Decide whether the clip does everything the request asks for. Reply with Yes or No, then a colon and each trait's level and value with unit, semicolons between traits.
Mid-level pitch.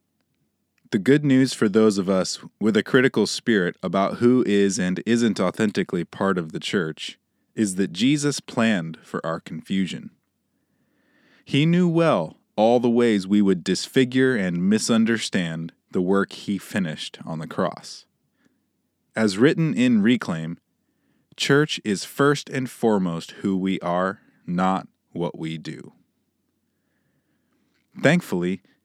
No: low, 110 Hz